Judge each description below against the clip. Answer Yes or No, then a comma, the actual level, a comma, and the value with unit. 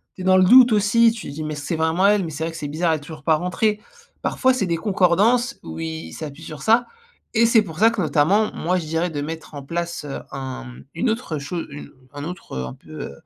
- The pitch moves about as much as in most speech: No, wide, 6.1 semitones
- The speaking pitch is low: No, medium, 165 Hz